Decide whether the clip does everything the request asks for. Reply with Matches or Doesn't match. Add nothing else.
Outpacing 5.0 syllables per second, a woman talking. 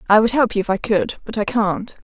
Matches